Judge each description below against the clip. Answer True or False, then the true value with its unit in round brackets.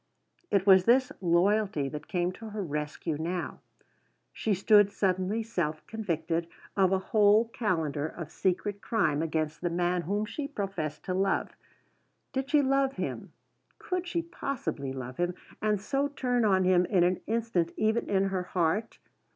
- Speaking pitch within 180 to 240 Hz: True (190 Hz)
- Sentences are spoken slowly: False (160 wpm)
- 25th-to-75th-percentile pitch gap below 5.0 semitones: True (4.3 semitones)